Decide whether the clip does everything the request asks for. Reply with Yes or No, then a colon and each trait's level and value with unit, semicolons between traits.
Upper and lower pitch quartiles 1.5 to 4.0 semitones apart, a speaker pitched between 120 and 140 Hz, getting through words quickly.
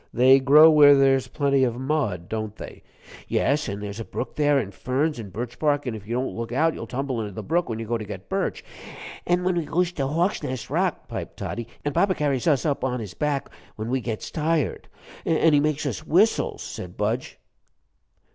No: average, 4.7 semitones; low, 135 Hz; fast, 210 wpm